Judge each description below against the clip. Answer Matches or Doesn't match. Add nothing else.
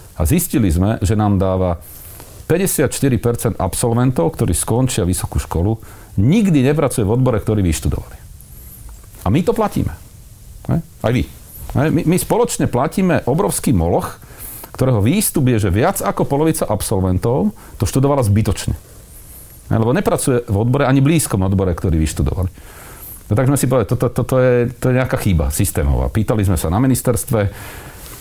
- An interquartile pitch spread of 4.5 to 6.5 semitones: Matches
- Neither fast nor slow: Matches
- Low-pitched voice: Matches